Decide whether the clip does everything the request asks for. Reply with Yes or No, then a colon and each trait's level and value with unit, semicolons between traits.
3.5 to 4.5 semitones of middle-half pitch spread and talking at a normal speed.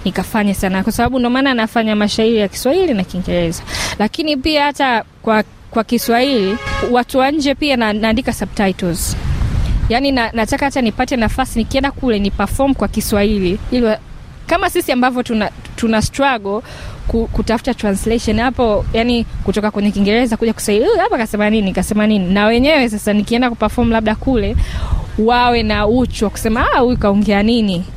No: average, 3.1 semitones; average, 120 wpm